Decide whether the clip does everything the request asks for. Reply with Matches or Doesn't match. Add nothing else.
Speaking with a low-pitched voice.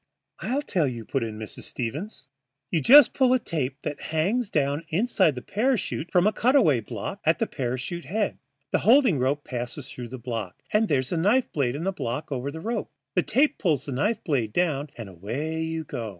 Doesn't match